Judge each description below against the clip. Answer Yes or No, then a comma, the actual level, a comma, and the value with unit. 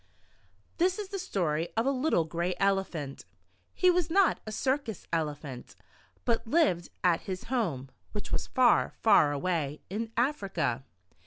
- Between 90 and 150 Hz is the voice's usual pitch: No, high, 195 Hz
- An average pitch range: No, wide, 8.7 semitones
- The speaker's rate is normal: Yes, average, 145 wpm